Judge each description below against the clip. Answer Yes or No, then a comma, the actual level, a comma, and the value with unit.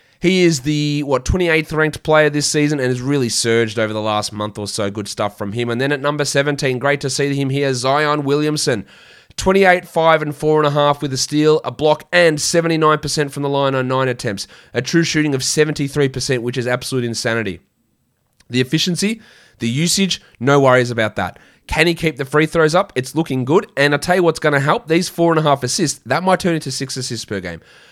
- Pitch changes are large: No, average, 3.7 semitones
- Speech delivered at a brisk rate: Yes, fast, 215 wpm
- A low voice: No, medium, 145 Hz